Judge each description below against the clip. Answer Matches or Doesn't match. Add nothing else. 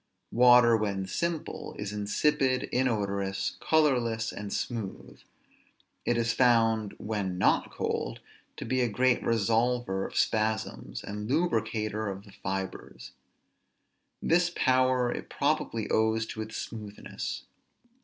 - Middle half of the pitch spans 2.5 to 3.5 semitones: Matches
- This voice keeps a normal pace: Doesn't match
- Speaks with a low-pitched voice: Matches